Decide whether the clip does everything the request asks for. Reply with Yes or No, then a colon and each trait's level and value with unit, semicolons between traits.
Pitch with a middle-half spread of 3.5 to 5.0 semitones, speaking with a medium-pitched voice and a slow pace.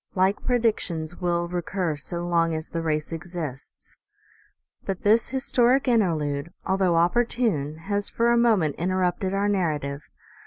Yes: average, 4.2 semitones; medium, 175 Hz; slow, 130 wpm